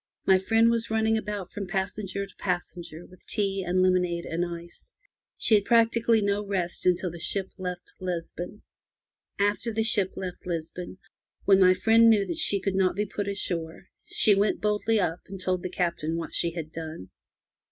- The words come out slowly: No, average, 180 wpm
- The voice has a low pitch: No, high, 190 Hz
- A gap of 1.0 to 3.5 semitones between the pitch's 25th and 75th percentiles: Yes, average, 2.9 semitones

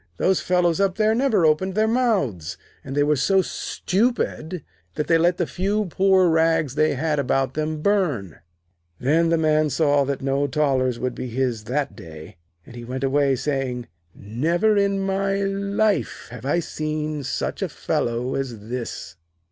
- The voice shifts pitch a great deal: Yes, wide, 6.2 semitones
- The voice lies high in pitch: No, medium, 155 Hz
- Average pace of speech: Yes, average, 165 wpm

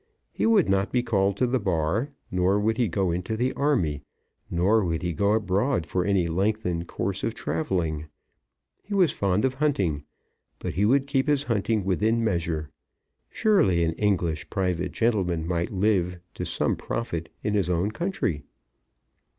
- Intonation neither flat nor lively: Yes, average, 4.9 semitones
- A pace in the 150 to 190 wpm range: Yes, average, 165 wpm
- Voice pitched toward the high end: No, low, 100 Hz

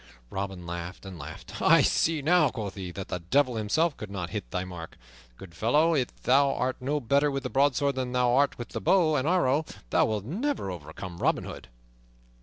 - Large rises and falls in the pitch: Yes, wide, 7.3 semitones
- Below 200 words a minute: No, fast, 205 wpm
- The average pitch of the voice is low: Yes, low, 125 Hz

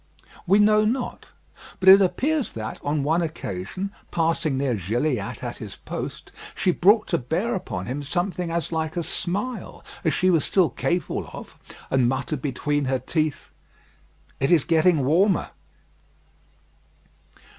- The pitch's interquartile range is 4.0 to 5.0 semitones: No, wide, 5.6 semitones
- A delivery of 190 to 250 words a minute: No, average, 145 wpm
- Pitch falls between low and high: Yes, medium, 160 Hz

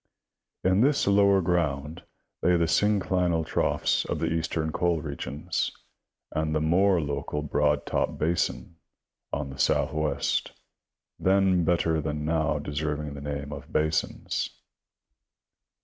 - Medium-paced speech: No, slow, 125 wpm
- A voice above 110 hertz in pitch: No, very low, 80 Hz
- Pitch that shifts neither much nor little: Yes, average, 3.0 semitones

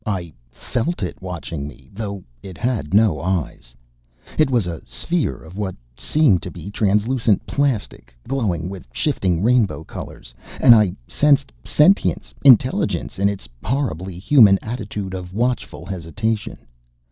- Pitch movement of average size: No, wide, 5.7 semitones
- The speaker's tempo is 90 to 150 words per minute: Yes, slow, 135 wpm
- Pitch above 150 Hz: No, low, 100 Hz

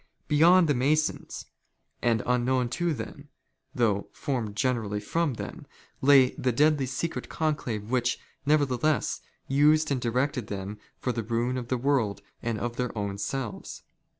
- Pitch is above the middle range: No, low, 125 Hz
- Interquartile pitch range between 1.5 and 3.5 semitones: No, average, 3.9 semitones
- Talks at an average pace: Yes, average, 145 wpm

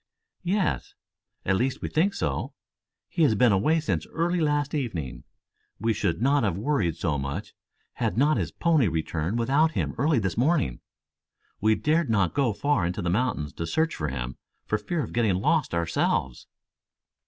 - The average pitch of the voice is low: Yes, low, 115 Hz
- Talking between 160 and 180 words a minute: Yes, average, 170 wpm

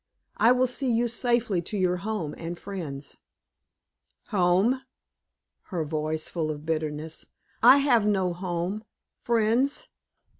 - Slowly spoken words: Yes, slow, 120 wpm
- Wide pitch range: Yes, wide, 6.3 semitones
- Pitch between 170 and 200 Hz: Yes, high, 190 Hz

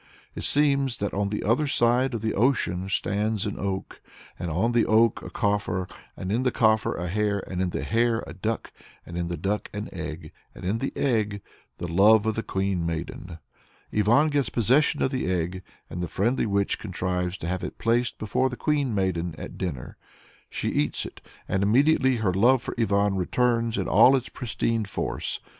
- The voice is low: Yes, low, 105 Hz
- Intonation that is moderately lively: Yes, average, 4.4 semitones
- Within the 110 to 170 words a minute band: No, average, 195 wpm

